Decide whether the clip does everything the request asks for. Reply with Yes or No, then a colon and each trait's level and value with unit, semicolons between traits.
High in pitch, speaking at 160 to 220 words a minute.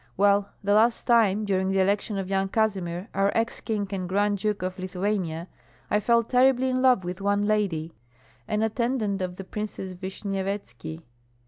Yes: high, 200 Hz; average, 165 wpm